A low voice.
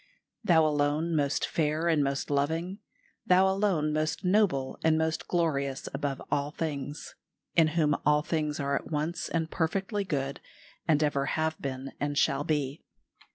No: medium, 155 Hz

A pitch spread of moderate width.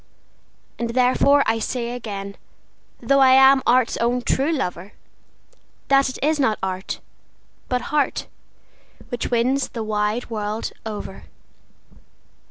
Yes: average, 3.7 semitones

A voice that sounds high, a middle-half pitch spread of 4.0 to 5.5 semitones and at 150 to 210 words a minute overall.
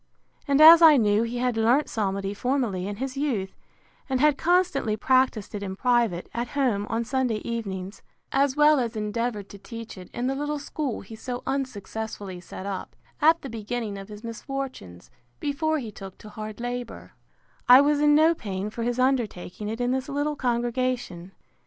Yes: high, 240 Hz; average, 4.6 semitones; average, 180 wpm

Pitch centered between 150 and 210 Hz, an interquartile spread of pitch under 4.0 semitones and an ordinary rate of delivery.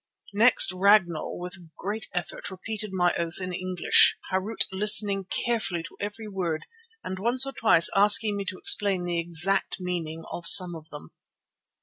Yes: high, 190 Hz; average, 2.9 semitones; average, 160 wpm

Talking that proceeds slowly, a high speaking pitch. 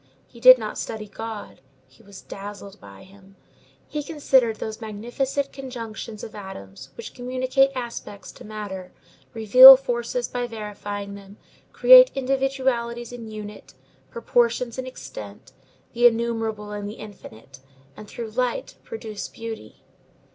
Yes: slow, 130 wpm; high, 225 Hz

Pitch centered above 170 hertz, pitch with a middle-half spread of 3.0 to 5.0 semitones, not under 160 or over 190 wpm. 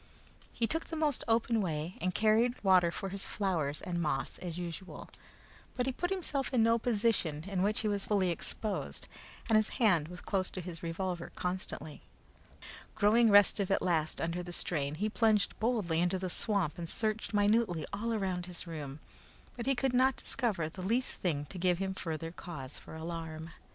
Yes: high, 190 Hz; average, 4.7 semitones; average, 180 wpm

